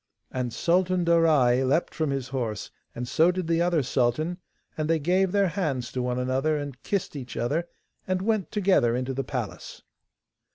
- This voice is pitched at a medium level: Yes, medium, 150 Hz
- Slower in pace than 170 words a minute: No, average, 175 wpm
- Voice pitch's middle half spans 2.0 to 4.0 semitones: No, wide, 5.6 semitones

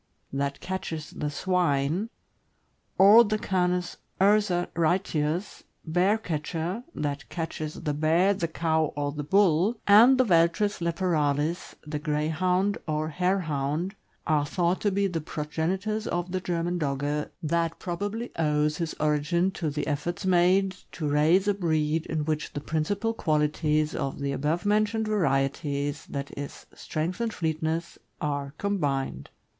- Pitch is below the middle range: No, medium, 165 Hz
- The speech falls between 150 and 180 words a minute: No, slow, 135 wpm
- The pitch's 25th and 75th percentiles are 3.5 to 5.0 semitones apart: Yes, average, 3.9 semitones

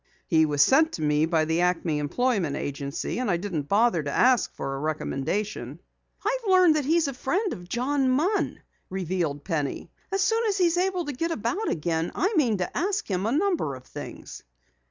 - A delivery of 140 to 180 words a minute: No, average, 195 wpm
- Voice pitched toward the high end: Yes, high, 215 Hz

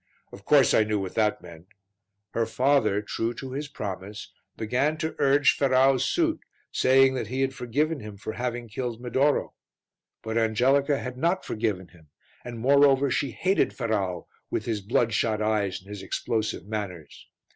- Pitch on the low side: Yes, low, 120 Hz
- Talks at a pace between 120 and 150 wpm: No, average, 160 wpm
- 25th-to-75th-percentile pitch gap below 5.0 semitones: Yes, average, 4.3 semitones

